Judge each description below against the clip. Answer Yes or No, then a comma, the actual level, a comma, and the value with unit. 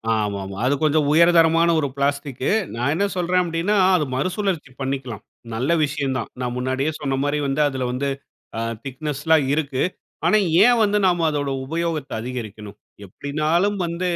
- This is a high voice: No, medium, 145 Hz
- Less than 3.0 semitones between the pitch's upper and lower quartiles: No, average, 4.2 semitones